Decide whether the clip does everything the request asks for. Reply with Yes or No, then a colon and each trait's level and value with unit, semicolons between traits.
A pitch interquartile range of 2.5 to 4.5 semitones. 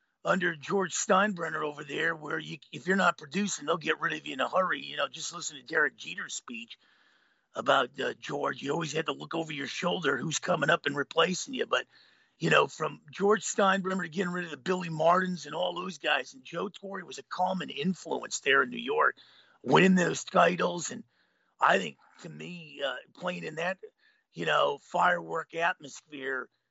Yes: average, 3.0 semitones